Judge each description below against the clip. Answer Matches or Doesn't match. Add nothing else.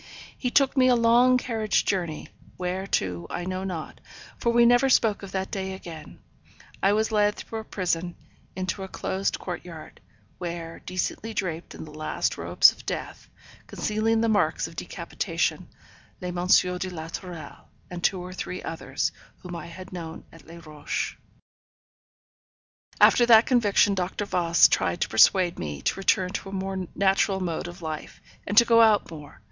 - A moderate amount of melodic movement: Matches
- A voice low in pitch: Doesn't match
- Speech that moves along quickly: Doesn't match